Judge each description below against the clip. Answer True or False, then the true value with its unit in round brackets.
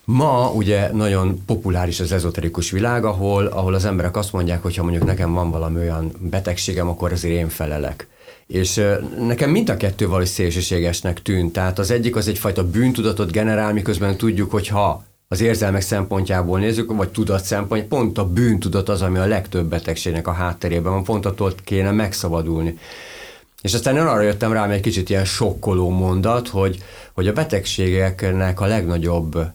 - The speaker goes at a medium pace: False (165 wpm)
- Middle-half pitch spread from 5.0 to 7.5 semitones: False (3.2 semitones)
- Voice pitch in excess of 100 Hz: False (95 Hz)